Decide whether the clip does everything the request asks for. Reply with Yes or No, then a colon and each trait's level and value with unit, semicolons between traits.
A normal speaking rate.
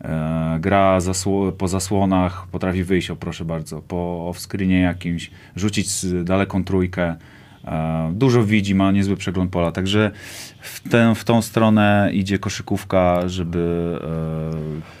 Yes: average, 125 wpm